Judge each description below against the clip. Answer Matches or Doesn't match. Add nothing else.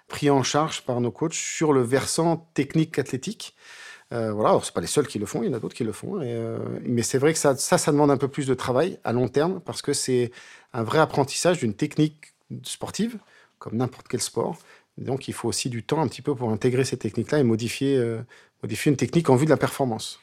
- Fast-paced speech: Matches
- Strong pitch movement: Doesn't match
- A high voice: Doesn't match